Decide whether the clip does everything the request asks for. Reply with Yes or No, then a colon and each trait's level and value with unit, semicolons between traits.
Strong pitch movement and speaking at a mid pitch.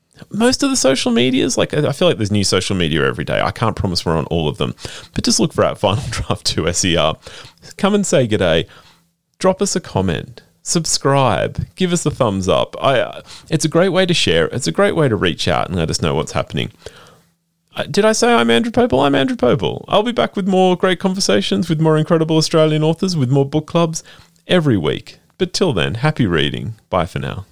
Yes: wide, 7.6 semitones; medium, 155 Hz